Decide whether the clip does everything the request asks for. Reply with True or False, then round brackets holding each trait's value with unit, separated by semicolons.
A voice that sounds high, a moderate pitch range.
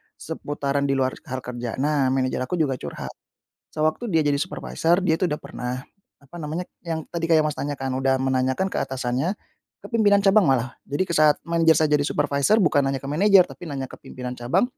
False (145 Hz; 4.0 semitones)